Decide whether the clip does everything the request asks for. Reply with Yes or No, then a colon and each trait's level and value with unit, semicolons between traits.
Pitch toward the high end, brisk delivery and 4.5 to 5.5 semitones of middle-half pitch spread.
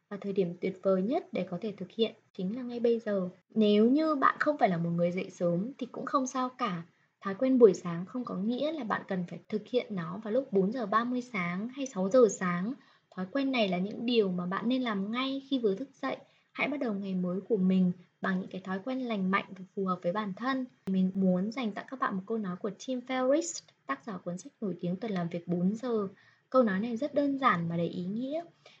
Yes: high, 210 Hz; fast, 255 wpm; average, 5.2 semitones